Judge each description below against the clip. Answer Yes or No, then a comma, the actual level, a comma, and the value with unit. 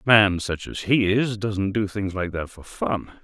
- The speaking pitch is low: Yes, low, 100 Hz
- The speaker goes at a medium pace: No, fast, 240 wpm